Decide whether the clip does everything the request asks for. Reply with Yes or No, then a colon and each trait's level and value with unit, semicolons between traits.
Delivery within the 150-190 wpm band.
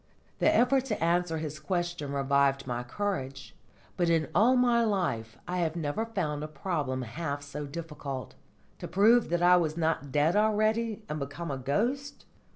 Yes: average, 165 wpm